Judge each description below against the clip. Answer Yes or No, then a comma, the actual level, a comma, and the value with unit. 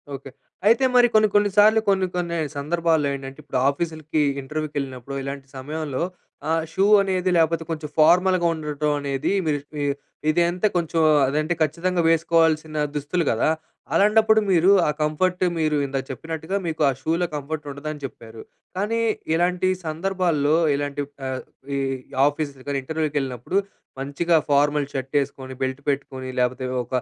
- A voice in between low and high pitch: Yes, medium, 155 Hz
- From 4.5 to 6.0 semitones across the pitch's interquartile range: No, average, 3.7 semitones